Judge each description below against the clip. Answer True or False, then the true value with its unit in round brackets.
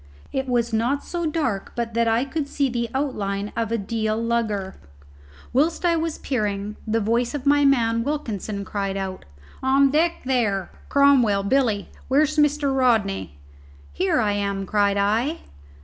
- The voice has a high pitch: True (235 Hz)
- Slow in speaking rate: False (155 wpm)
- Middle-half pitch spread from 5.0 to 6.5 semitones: True (5.3 semitones)